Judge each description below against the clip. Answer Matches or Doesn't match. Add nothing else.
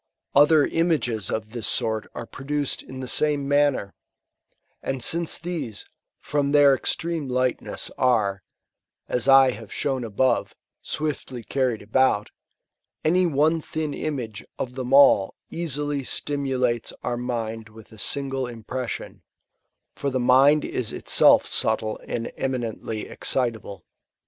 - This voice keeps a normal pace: Doesn't match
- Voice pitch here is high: Doesn't match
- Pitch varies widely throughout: Doesn't match